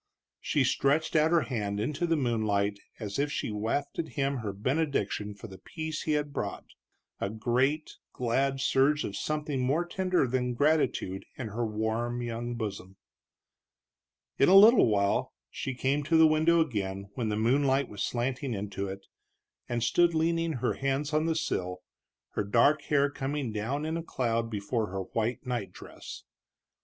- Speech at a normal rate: Yes, average, 165 wpm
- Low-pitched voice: Yes, low, 125 Hz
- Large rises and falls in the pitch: Yes, wide, 5.7 semitones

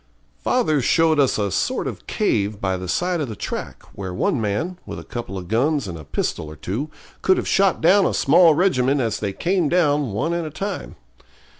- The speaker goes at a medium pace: No, fast, 210 wpm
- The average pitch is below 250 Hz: Yes, medium, 140 Hz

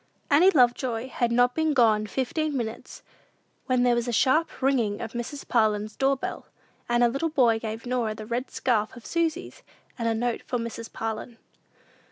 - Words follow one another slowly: No, average, 175 wpm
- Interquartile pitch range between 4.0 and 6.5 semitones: No, average, 2.9 semitones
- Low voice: No, high, 240 Hz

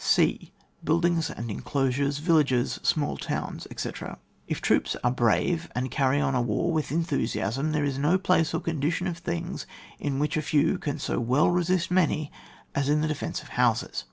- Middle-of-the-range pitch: Yes, medium, 145 Hz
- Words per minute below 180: No, average, 185 wpm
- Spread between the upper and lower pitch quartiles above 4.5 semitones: No, average, 3.7 semitones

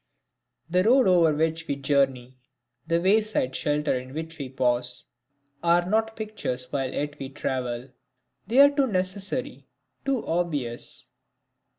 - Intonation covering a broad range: Yes, wide, 6.9 semitones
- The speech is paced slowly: Yes, slow, 130 wpm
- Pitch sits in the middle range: Yes, medium, 160 Hz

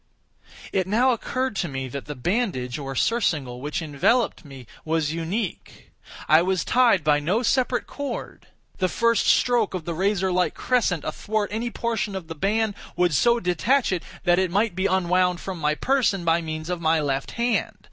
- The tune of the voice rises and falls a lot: Yes, wide, 6.1 semitones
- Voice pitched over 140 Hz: Yes, medium, 185 Hz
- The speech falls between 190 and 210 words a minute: No, average, 175 wpm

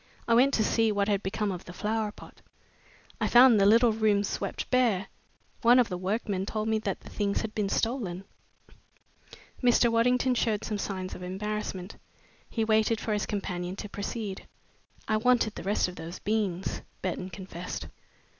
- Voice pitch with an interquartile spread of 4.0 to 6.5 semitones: No, average, 2.8 semitones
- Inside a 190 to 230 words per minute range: No, average, 175 wpm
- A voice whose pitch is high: Yes, high, 210 Hz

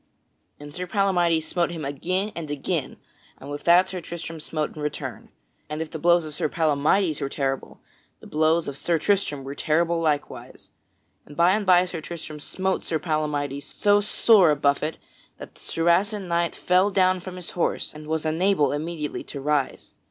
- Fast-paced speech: No, average, 180 wpm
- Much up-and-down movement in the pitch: No, average, 3.3 semitones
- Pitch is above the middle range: No, medium, 165 Hz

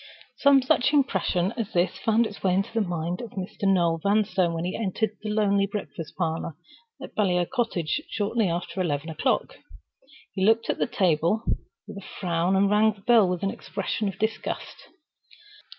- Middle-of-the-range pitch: No, high, 195 Hz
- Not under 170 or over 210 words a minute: Yes, average, 175 wpm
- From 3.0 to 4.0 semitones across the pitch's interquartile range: Yes, average, 3.7 semitones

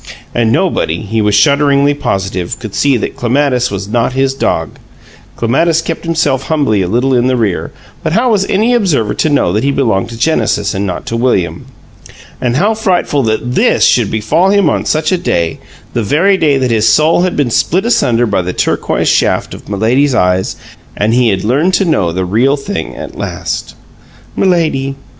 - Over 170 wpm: Yes, average, 190 wpm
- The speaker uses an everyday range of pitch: No, wide, 6.6 semitones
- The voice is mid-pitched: No, low, 130 Hz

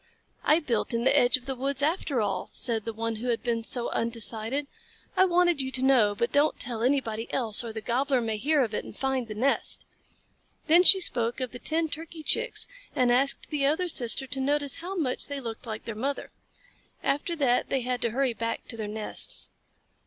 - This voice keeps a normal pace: No, fast, 210 wpm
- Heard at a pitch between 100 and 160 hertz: No, very high, 255 Hz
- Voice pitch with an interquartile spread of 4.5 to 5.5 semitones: No, average, 3.8 semitones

